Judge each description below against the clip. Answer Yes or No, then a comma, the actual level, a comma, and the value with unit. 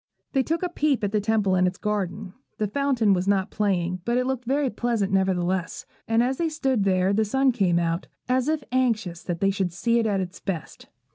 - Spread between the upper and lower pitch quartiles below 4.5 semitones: No, average, 5.2 semitones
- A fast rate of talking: Yes, fast, 220 wpm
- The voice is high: Yes, high, 210 Hz